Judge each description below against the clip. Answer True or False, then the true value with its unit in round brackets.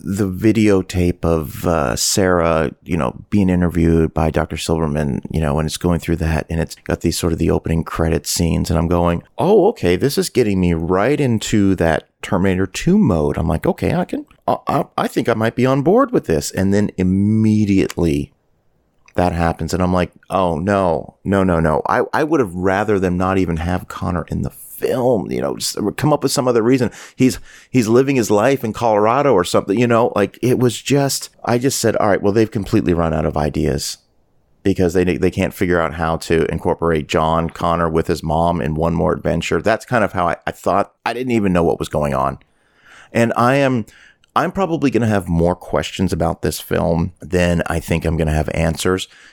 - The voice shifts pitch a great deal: False (4.4 semitones)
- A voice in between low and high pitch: False (90 Hz)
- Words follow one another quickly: True (215 wpm)